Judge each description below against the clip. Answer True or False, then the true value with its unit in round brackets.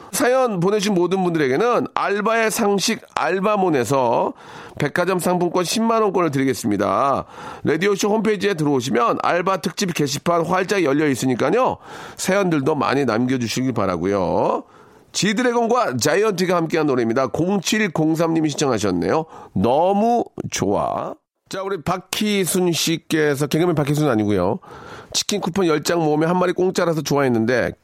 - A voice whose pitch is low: False (175 Hz)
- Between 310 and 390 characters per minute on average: True (345 characters per minute)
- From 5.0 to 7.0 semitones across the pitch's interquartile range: True (5.3 semitones)